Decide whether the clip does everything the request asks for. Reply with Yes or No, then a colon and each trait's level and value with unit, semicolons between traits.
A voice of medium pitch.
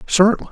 No: high, 210 Hz